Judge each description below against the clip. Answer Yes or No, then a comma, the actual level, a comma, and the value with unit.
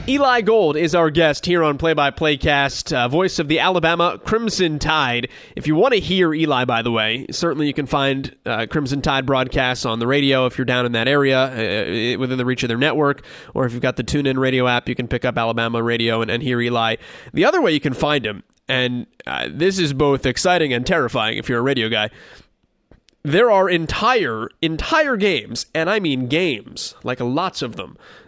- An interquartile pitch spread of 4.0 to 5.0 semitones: Yes, average, 4.4 semitones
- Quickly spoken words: Yes, fast, 215 wpm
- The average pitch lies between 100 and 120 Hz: No, medium, 140 Hz